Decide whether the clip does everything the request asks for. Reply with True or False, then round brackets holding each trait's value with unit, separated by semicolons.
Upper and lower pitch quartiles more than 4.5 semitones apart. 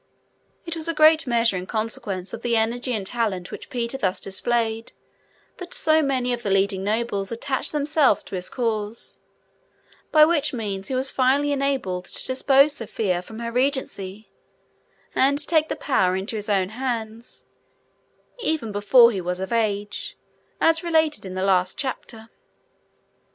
True (5.4 semitones)